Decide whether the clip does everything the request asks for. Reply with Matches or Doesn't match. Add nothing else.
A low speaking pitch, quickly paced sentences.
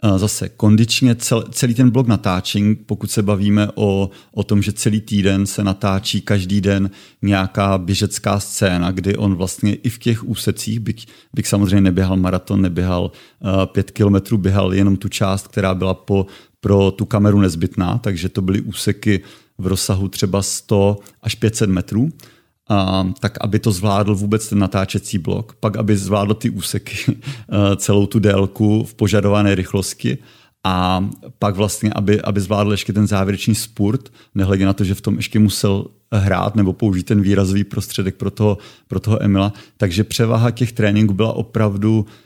Doesn't match